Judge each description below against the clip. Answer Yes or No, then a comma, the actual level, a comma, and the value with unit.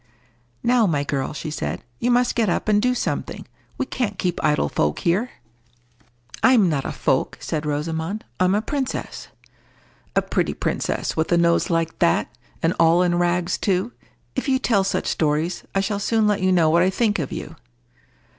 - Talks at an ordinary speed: Yes, average, 180 wpm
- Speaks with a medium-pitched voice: Yes, medium, 180 Hz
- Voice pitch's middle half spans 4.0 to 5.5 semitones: Yes, average, 4.8 semitones